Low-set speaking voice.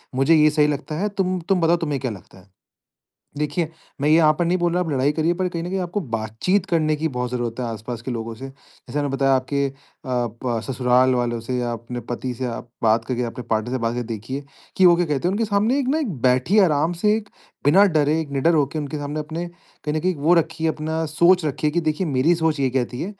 No: medium, 150 Hz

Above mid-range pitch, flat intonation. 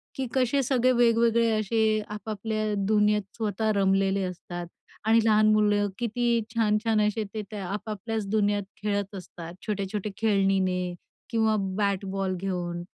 Yes: high, 210 Hz; narrow, 2.3 semitones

